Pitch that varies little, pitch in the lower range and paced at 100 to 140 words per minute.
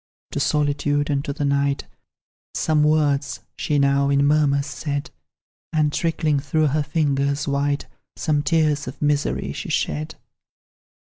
No: narrow, 1.3 semitones; medium, 145 Hz; slow, 135 wpm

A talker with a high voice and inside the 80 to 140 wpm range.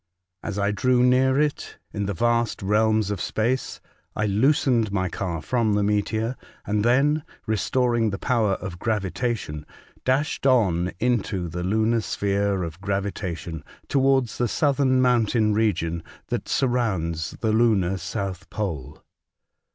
No: low, 105 Hz; slow, 135 wpm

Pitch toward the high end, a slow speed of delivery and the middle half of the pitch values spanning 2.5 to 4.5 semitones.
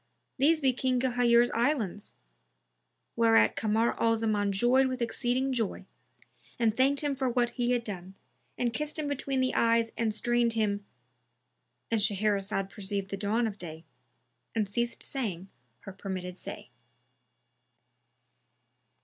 Yes: high, 225 Hz; slow, 130 wpm; average, 3.8 semitones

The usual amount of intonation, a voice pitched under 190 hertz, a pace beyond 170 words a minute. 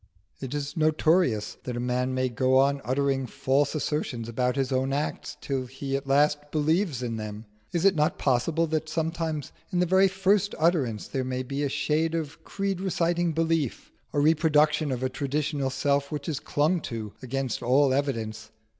Yes: average, 3.6 semitones; medium, 140 Hz; average, 180 wpm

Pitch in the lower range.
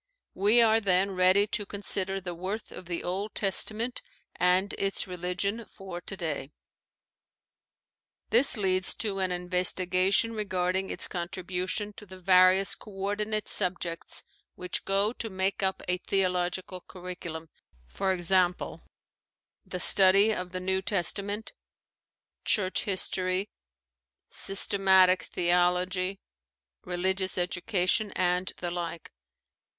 No: medium, 185 Hz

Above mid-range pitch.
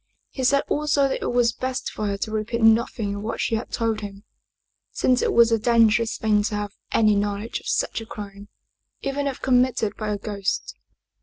Yes: high, 225 Hz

